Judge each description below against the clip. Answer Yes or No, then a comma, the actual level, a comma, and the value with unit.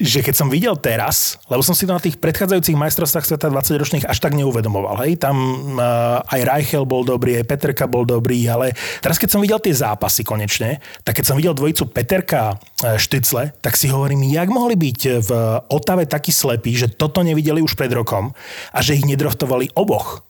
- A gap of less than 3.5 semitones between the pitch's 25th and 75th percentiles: No, average, 4.5 semitones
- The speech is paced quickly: Yes, fast, 195 wpm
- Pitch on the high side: No, medium, 140 Hz